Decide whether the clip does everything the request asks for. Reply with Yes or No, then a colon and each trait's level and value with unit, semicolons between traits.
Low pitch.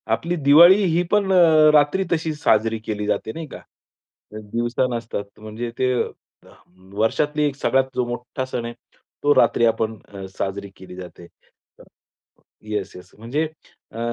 Yes: low, 120 Hz